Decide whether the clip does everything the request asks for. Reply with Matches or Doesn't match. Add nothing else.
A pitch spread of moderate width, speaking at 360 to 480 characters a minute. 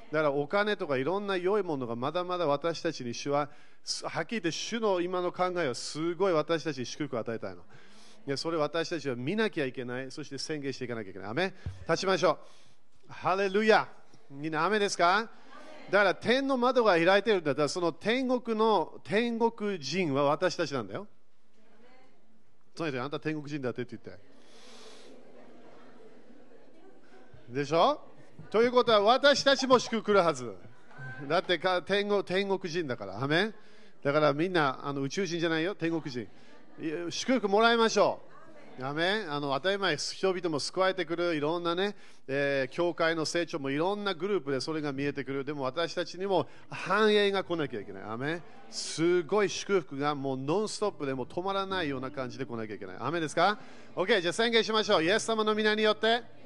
Doesn't match